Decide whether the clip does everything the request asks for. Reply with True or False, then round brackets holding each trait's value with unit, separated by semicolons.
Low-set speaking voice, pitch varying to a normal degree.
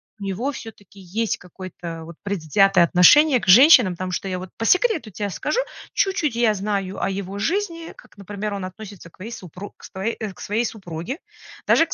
False (200 Hz; 3.8 semitones)